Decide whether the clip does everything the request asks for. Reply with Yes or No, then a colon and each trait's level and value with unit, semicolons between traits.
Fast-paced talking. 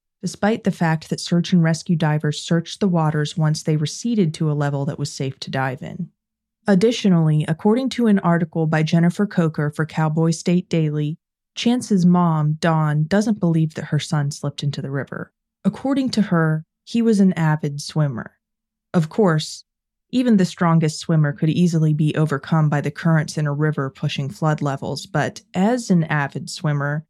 No: average, 175 wpm